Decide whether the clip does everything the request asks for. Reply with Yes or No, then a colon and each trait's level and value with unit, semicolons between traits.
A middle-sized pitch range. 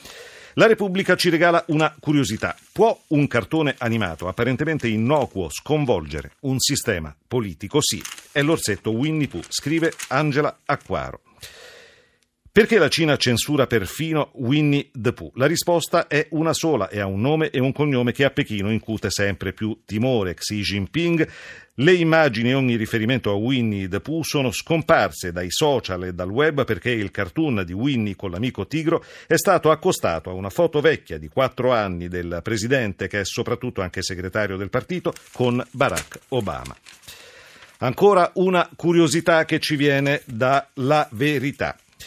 No: wide, 6.8 semitones